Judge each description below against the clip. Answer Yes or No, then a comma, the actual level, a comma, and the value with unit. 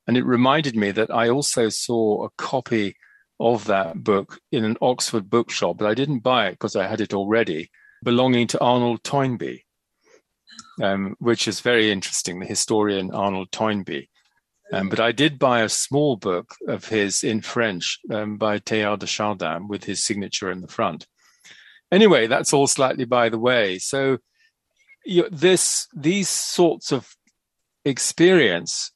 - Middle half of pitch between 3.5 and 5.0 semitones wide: Yes, average, 4.1 semitones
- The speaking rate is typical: Yes, average, 160 wpm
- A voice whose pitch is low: Yes, low, 115 Hz